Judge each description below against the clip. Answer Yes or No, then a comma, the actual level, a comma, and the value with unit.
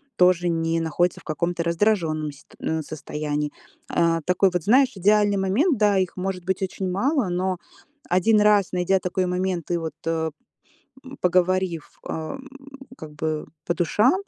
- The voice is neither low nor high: Yes, medium, 180 Hz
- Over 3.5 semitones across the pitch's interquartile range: No, average, 2.8 semitones